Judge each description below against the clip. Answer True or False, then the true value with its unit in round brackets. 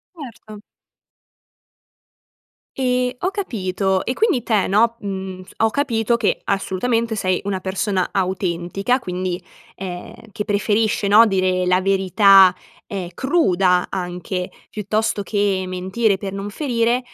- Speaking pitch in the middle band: False (200 Hz)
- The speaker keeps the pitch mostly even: False (3.5 semitones)